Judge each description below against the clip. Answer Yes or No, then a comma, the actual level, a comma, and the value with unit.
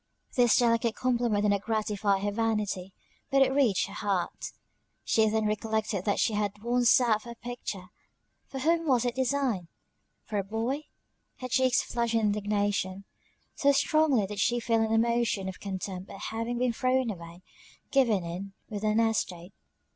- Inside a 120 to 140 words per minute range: No, average, 170 wpm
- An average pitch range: Yes, average, 3.2 semitones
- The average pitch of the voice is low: No, high, 220 Hz